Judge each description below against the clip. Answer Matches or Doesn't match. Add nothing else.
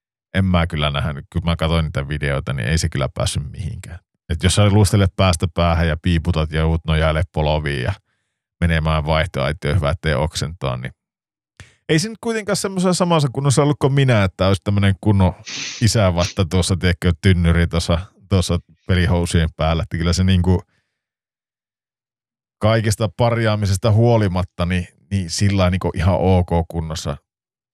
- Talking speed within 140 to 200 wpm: Matches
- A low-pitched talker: Matches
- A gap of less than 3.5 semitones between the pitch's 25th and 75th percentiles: Doesn't match